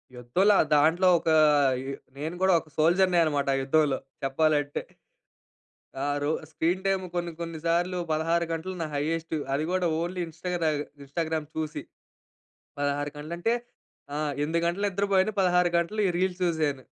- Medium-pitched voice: Yes, medium, 165 Hz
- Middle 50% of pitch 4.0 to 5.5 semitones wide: No, average, 3.0 semitones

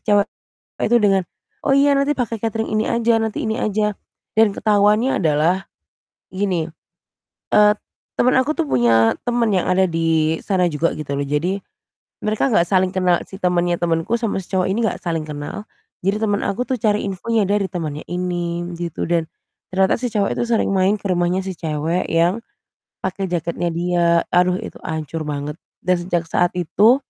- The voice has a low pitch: No, medium, 185 Hz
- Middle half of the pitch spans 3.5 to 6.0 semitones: Yes, average, 4.0 semitones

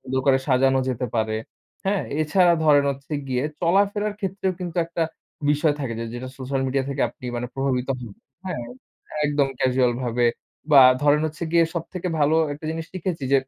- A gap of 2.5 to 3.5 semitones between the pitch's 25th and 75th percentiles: No, average, 4.5 semitones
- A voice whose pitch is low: No, medium, 145 Hz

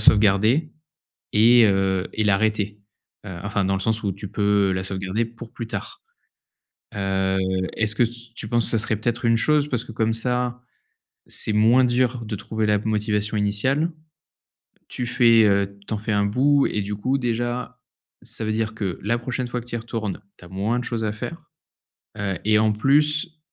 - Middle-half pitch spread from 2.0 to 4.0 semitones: Yes, average, 2.8 semitones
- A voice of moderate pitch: No, low, 110 Hz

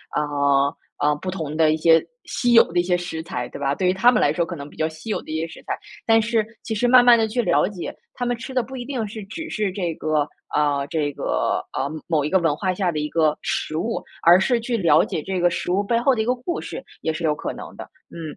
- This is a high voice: No, medium, 175 Hz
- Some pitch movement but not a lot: No, wide, 6.5 semitones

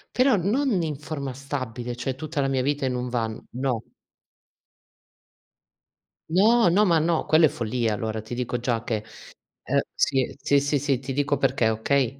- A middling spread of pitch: Yes, average, 3.9 semitones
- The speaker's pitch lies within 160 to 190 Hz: No, low, 135 Hz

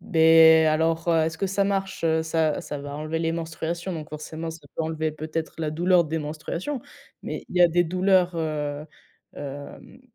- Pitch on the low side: No, medium, 160 Hz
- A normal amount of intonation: No, narrow, 1.8 semitones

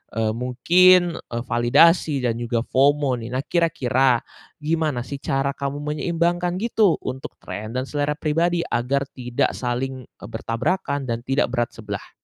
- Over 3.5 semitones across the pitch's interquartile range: Yes, average, 4.8 semitones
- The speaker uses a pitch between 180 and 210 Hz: No, low, 135 Hz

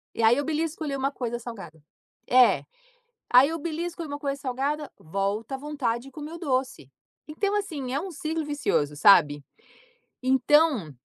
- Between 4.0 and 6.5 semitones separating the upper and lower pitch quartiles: Yes, average, 4.5 semitones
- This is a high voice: Yes, very high, 275 Hz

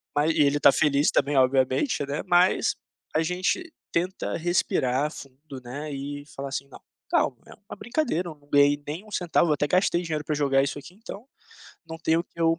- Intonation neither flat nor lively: Yes, average, 3.7 semitones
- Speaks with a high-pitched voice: No, medium, 150 Hz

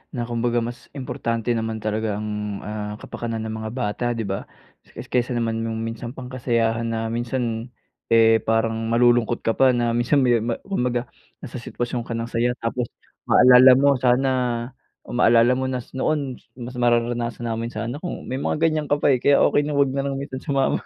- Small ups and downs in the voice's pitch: Yes, narrow, 2.2 semitones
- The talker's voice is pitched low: Yes, low, 120 Hz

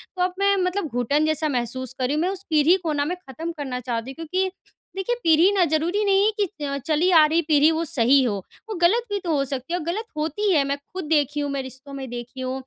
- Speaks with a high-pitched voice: Yes, very high, 310 Hz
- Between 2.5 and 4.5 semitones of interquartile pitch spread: No, average, 5.0 semitones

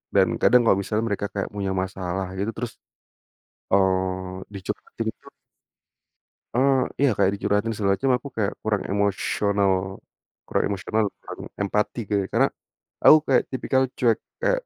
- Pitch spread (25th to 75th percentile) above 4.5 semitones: No, average, 3.1 semitones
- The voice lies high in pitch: No, low, 100 Hz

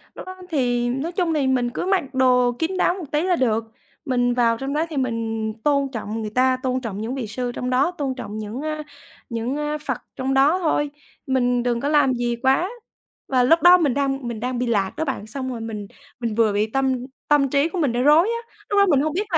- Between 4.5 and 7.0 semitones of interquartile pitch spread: No, average, 3.9 semitones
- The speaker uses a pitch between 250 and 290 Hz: Yes, very high, 260 Hz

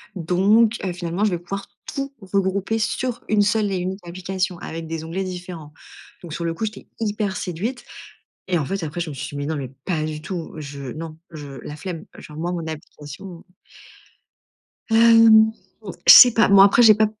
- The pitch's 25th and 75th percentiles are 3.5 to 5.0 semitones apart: Yes, average, 4.4 semitones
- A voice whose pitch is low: No, medium, 180 Hz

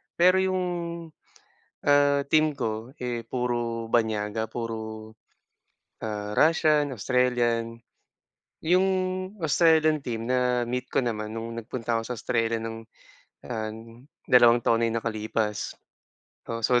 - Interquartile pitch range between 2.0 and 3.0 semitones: No, average, 4.1 semitones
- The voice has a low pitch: Yes, low, 120 Hz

